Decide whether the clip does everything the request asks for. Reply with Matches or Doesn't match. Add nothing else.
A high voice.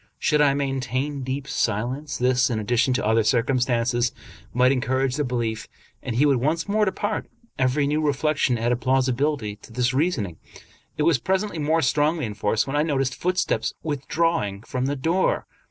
Doesn't match